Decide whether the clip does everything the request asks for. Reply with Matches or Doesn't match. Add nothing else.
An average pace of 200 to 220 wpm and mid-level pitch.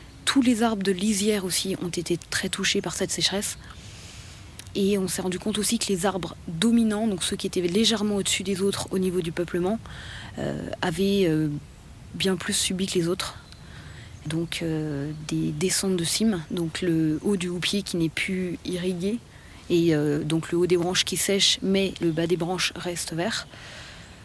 Doesn't match